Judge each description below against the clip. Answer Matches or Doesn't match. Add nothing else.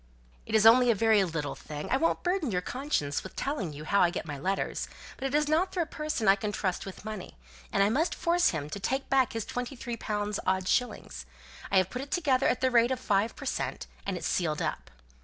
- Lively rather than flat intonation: Matches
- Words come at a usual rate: Doesn't match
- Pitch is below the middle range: Doesn't match